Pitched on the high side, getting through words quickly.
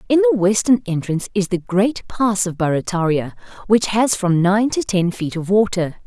No: high, 200 Hz; average, 190 wpm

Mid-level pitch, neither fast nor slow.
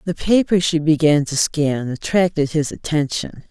Yes: medium, 155 Hz; average, 155 wpm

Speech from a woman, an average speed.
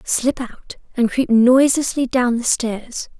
Yes: female; average, 150 wpm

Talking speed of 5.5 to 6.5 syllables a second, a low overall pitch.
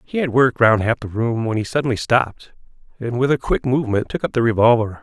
Yes: 6.3 syllables/s; low, 120 Hz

